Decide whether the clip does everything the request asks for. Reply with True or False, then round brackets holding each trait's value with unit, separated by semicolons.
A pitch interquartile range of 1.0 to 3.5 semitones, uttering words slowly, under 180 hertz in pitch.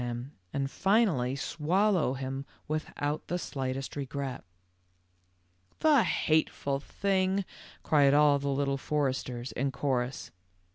True (2.8 semitones; 110 wpm; 140 Hz)